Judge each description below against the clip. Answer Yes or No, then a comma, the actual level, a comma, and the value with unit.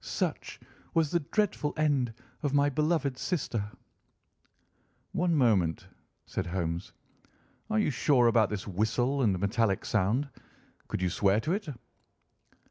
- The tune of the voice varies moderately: No, wide, 7.0 semitones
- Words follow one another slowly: Yes, slow, 125 wpm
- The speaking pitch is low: Yes, low, 125 Hz